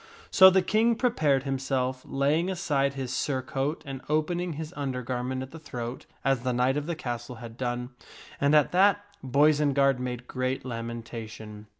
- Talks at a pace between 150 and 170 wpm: Yes, average, 165 wpm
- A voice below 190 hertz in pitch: Yes, low, 135 Hz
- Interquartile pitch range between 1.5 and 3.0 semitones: No, average, 3.4 semitones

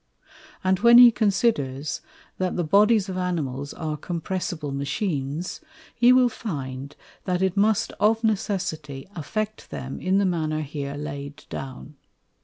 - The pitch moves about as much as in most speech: No, wide, 6.4 semitones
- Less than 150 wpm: Yes, slow, 135 wpm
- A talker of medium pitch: Yes, medium, 175 Hz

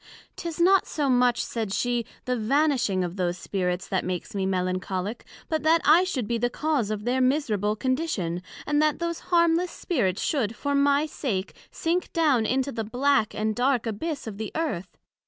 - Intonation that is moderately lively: No, wide, 6.6 semitones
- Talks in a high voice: Yes, high, 245 Hz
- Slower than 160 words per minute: No, average, 180 wpm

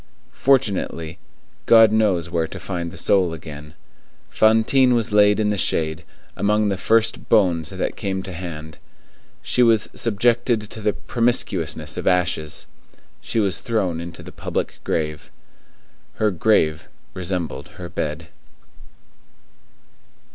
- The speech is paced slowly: Yes, slow, 125 wpm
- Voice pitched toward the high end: No, very low, 95 Hz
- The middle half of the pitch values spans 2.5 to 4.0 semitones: No, average, 5.0 semitones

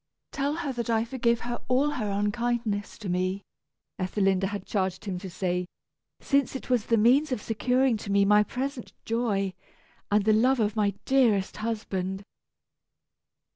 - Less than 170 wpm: Yes, average, 160 wpm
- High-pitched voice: Yes, high, 215 Hz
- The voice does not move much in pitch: No, average, 3.7 semitones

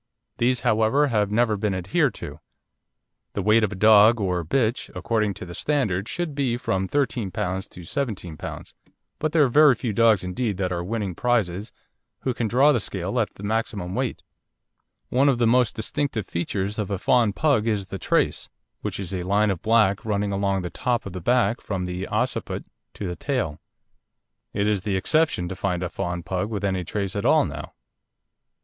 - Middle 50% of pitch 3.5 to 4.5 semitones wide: Yes, average, 4.1 semitones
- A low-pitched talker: Yes, low, 105 Hz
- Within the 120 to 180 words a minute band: No, average, 195 wpm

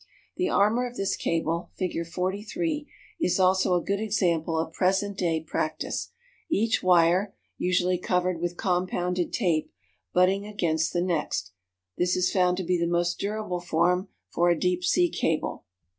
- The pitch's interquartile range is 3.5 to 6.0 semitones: No, narrow, 2.4 semitones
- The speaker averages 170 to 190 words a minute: No, average, 155 wpm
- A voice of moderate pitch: Yes, medium, 180 Hz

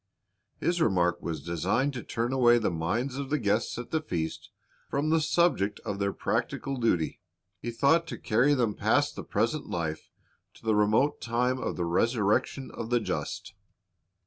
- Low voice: Yes, low, 115 Hz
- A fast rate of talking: No, average, 170 wpm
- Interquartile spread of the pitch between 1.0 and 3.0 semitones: No, wide, 5.5 semitones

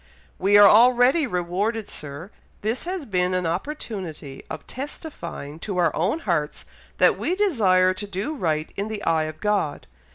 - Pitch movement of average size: No, wide, 5.8 semitones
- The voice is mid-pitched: No, high, 195 Hz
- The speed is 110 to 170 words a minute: Yes, average, 160 wpm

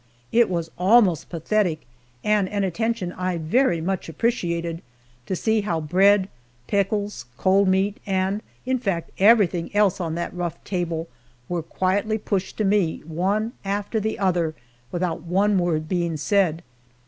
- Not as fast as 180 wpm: Yes, average, 145 wpm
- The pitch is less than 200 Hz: Yes, medium, 185 Hz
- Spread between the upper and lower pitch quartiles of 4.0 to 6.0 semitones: No, average, 3.3 semitones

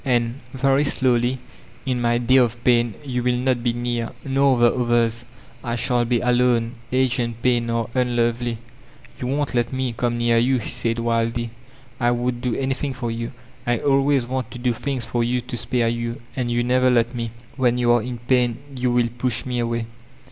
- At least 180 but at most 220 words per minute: Yes, fast, 205 wpm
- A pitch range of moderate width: No, narrow, 1.3 semitones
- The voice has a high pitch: No, low, 120 Hz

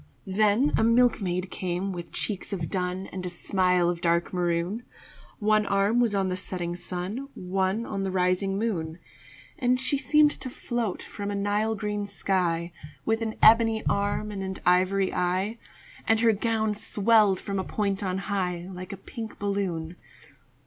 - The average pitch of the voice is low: No, high, 195 Hz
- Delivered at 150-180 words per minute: Yes, average, 165 wpm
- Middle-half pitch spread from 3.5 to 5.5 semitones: No, average, 3.1 semitones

